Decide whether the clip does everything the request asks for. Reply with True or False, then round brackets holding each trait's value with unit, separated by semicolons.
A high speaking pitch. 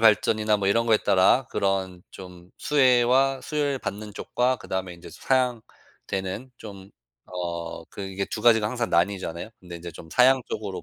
False (100 Hz)